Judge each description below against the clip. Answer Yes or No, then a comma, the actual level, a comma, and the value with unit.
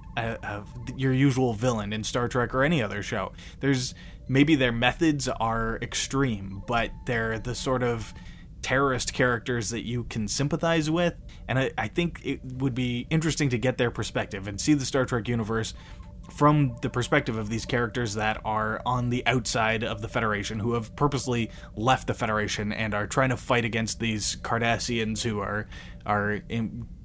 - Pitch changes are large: No, average, 3.2 semitones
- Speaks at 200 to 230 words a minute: No, average, 175 wpm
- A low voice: Yes, low, 120 Hz